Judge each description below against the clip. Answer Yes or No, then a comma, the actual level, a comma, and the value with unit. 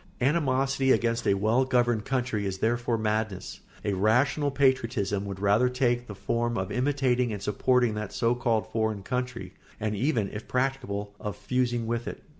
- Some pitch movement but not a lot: Yes, average, 3.3 semitones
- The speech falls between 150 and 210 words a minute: Yes, average, 165 wpm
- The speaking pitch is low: Yes, low, 120 Hz